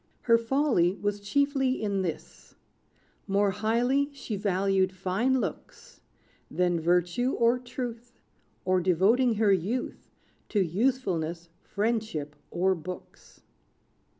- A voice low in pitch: No, high, 205 Hz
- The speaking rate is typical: No, slow, 105 wpm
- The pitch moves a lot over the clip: No, average, 4.9 semitones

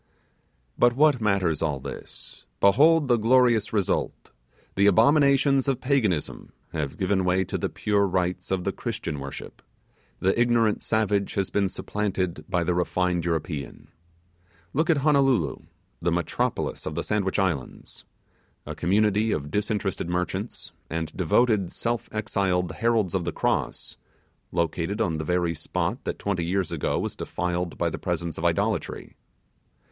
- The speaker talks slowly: No, average, 145 wpm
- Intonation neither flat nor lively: Yes, average, 4.3 semitones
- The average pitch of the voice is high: No, very low, 95 Hz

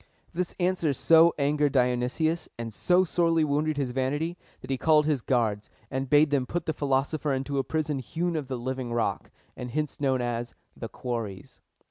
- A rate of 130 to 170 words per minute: No, average, 185 wpm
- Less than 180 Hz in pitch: Yes, medium, 140 Hz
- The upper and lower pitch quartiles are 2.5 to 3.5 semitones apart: No, average, 3.9 semitones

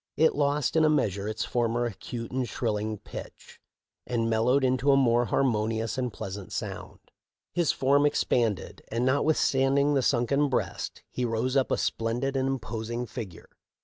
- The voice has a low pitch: Yes, low, 125 Hz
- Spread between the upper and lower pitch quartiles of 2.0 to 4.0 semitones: Yes, average, 3.3 semitones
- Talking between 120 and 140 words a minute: No, average, 165 wpm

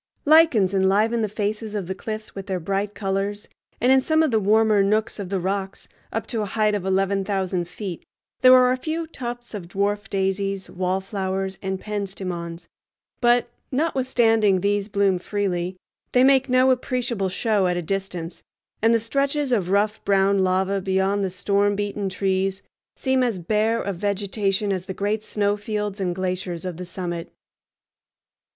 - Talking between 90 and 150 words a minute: No, average, 170 wpm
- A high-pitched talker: Yes, high, 200 Hz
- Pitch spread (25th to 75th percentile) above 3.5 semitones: No, narrow, 2.6 semitones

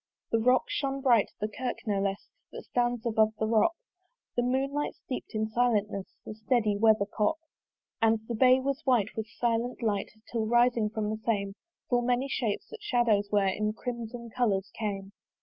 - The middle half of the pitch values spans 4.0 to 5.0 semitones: No, average, 2.7 semitones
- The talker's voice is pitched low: No, high, 225 Hz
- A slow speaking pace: No, average, 170 wpm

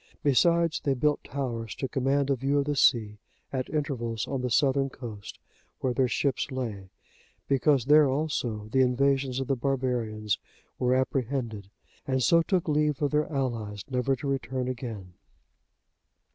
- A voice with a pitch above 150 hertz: No, low, 130 Hz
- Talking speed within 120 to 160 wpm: Yes, average, 155 wpm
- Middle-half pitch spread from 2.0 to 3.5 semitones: Yes, average, 2.8 semitones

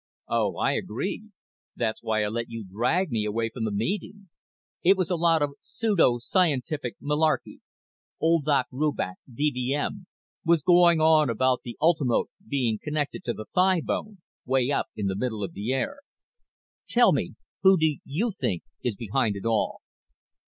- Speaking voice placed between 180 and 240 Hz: No, medium, 140 Hz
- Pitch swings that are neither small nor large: No, wide, 6.5 semitones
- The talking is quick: No, average, 160 wpm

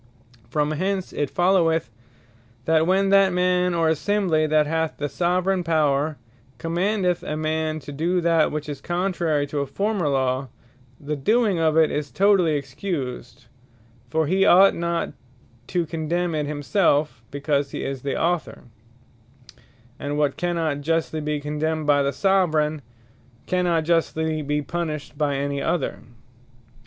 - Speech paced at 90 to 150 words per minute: Yes, average, 145 wpm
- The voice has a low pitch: No, medium, 160 Hz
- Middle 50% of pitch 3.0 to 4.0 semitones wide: Yes, average, 3.3 semitones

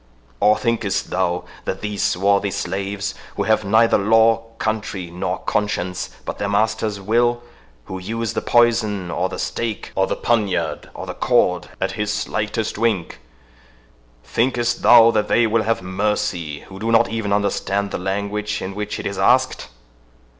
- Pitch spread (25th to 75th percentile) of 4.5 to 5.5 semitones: No, average, 3.1 semitones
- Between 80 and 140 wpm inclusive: No, average, 155 wpm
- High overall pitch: No, low, 100 Hz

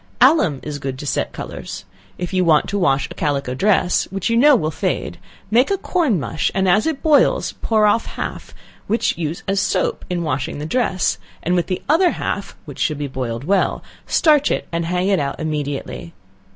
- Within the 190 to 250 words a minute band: Yes, average, 200 wpm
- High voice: No, medium, 180 Hz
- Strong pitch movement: Yes, wide, 6.5 semitones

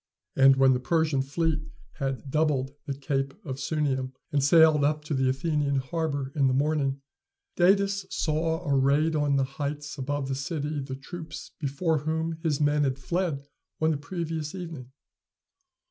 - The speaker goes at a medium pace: Yes, average, 160 wpm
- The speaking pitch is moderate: Yes, medium, 145 Hz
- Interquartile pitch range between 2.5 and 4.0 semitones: Yes, average, 2.8 semitones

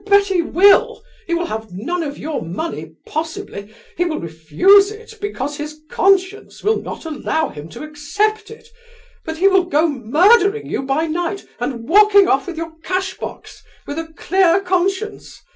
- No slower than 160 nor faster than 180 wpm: Yes, average, 170 wpm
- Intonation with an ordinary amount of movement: Yes, average, 4.9 semitones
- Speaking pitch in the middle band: No, very high, 340 Hz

